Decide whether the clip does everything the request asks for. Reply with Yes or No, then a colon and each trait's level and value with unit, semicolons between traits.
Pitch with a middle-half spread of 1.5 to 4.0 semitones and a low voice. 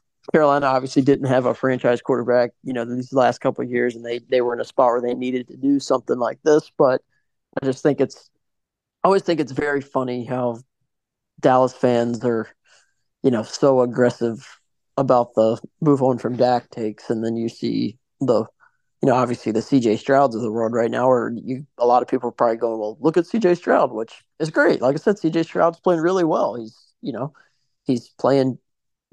Yes: average, 2.8 semitones; low, 125 Hz